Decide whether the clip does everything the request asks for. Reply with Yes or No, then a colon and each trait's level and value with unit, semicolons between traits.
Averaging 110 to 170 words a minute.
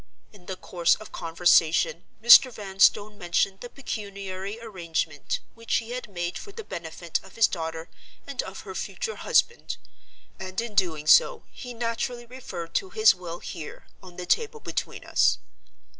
Yes: average, 155 wpm